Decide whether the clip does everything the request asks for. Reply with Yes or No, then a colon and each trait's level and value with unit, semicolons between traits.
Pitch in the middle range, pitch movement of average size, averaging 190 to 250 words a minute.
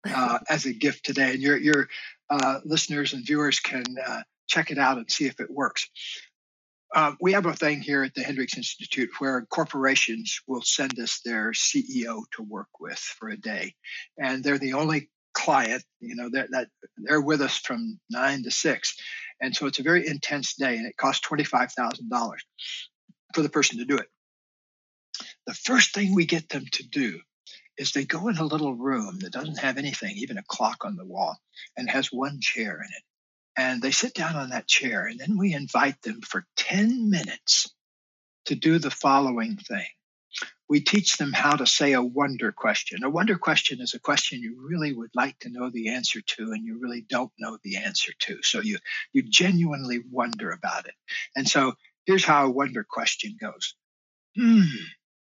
No: medium, 145 Hz; wide, 6.2 semitones; average, 195 wpm